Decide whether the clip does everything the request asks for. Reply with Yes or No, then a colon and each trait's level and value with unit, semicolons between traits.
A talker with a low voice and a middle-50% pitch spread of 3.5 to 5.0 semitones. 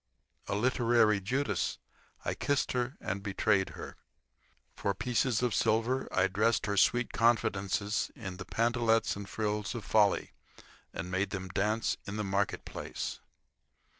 No: low, 105 Hz; average, 2.9 semitones